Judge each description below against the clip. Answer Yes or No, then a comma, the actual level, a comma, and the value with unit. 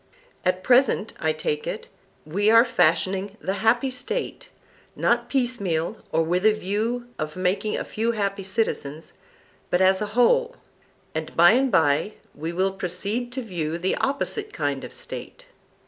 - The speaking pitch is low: No, high, 200 Hz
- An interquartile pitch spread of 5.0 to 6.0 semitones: Yes, average, 5.3 semitones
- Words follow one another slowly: No, average, 155 wpm